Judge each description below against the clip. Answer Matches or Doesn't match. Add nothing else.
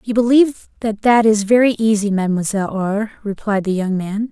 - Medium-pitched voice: Doesn't match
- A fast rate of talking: Doesn't match